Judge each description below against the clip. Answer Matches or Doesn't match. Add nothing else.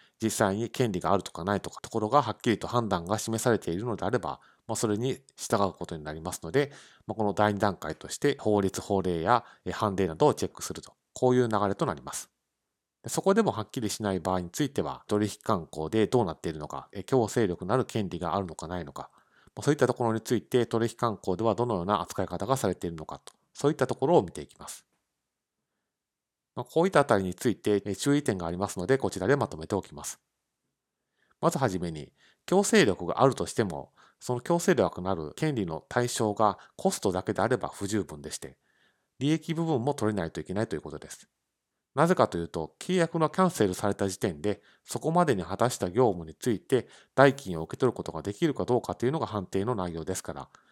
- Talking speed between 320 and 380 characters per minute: Doesn't match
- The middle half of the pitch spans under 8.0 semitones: Matches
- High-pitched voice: Doesn't match